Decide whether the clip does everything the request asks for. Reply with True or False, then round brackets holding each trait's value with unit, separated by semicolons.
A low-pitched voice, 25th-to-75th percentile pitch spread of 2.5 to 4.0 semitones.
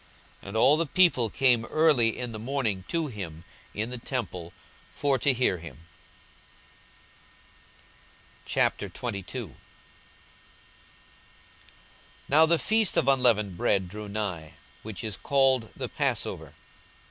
False (115 Hz; 5.4 semitones)